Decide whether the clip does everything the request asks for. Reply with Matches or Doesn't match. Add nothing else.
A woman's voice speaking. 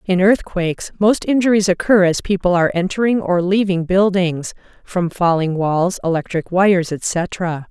Matches